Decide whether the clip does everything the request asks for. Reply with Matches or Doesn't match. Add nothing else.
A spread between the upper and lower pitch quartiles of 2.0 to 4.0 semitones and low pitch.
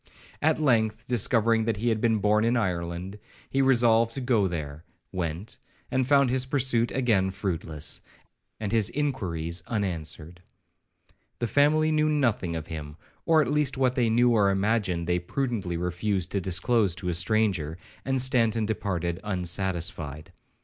Doesn't match